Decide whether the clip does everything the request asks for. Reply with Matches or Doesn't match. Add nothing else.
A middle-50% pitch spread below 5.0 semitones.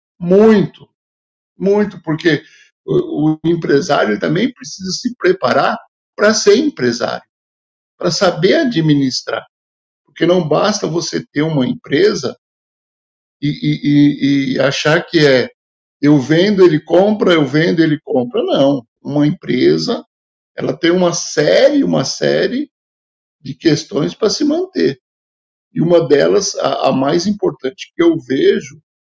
Doesn't match